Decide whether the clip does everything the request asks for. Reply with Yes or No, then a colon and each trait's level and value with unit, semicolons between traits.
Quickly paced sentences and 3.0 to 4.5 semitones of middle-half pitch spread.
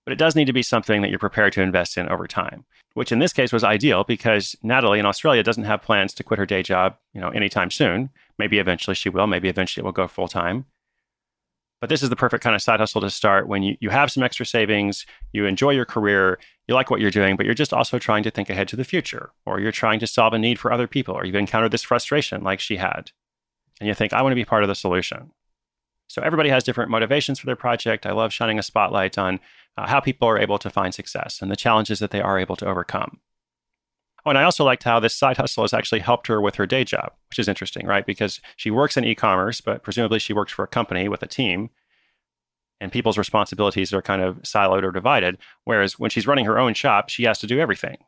Yes: fast, 255 wpm; average, 3.8 semitones